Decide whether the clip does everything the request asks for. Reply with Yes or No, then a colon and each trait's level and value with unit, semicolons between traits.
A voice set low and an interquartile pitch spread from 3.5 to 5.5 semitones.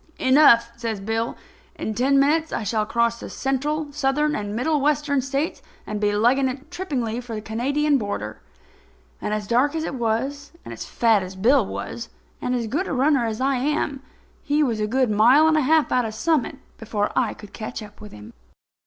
No: very high, 250 Hz; average, 4.5 semitones